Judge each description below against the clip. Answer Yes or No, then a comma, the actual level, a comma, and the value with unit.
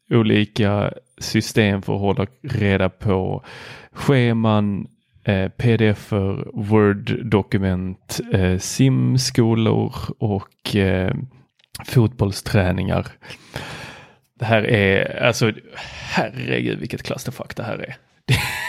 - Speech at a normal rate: No, slow, 85 wpm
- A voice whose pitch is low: Yes, low, 105 Hz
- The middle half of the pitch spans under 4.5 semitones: Yes, average, 3.5 semitones